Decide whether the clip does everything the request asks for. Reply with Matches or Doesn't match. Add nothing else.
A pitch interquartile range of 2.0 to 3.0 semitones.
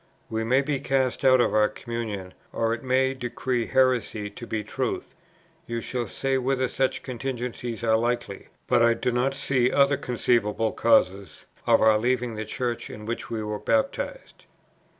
Matches